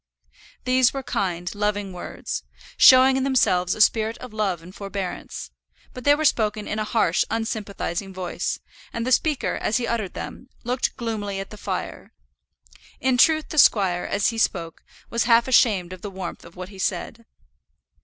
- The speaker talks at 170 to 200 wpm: Yes, average, 175 wpm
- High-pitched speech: Yes, high, 215 Hz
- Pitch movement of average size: Yes, average, 4.4 semitones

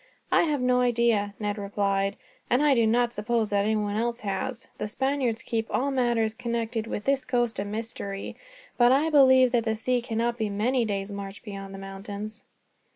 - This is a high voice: Yes, high, 225 Hz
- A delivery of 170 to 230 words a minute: Yes, average, 185 wpm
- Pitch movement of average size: Yes, average, 3.2 semitones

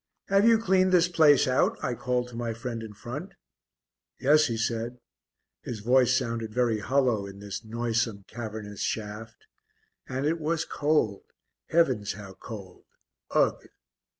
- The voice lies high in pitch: No, low, 120 Hz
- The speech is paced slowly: No, average, 145 wpm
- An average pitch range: Yes, average, 4.8 semitones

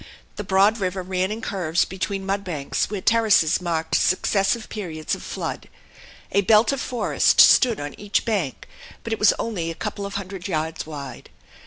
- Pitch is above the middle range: Yes, high, 195 Hz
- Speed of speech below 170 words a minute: No, average, 175 wpm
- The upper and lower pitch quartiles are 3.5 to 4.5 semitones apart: Yes, average, 3.9 semitones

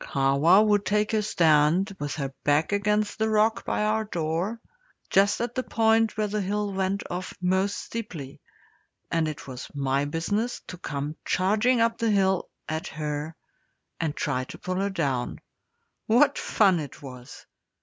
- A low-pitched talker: No, high, 190 Hz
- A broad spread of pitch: Yes, wide, 5.8 semitones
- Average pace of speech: Yes, average, 160 wpm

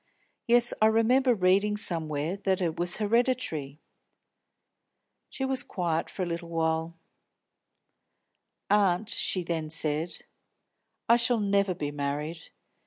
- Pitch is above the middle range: No, medium, 180 Hz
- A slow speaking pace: Yes, slow, 110 wpm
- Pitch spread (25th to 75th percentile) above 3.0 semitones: Yes, average, 5.1 semitones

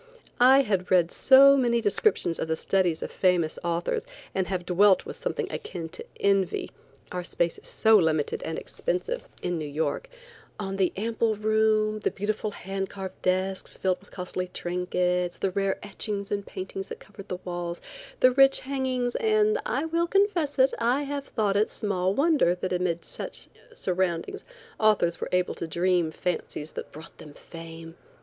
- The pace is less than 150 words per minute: No, average, 170 wpm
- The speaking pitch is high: Yes, high, 195 Hz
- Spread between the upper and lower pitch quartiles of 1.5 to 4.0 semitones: No, average, 4.6 semitones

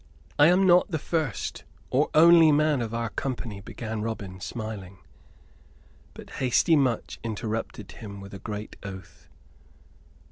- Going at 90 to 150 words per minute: Yes, slow, 135 wpm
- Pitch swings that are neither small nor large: No, wide, 6.5 semitones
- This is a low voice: Yes, low, 115 Hz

